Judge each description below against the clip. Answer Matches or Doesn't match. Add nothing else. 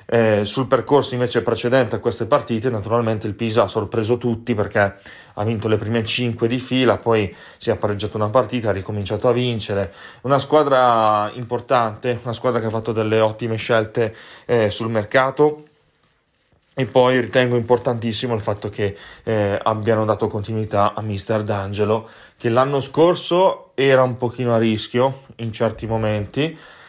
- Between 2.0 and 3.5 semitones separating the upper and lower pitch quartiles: Matches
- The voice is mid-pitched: Doesn't match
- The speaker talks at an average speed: Matches